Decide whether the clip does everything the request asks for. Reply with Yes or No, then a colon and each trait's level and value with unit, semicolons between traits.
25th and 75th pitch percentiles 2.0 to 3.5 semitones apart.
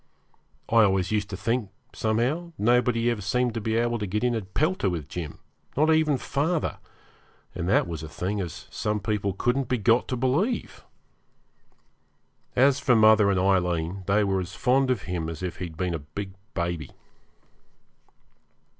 No: average, 5.1 semitones